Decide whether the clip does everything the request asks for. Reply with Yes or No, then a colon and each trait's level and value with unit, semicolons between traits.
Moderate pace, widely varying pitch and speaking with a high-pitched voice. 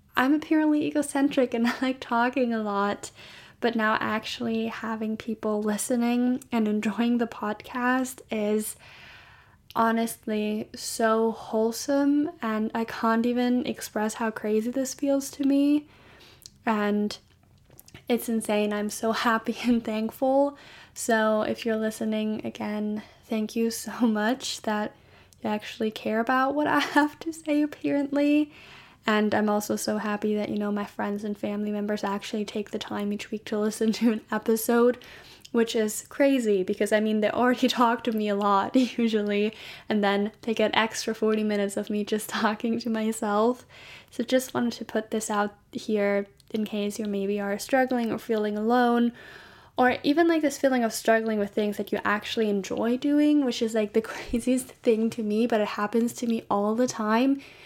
No: average, 165 wpm; narrow, 2.6 semitones; high, 225 Hz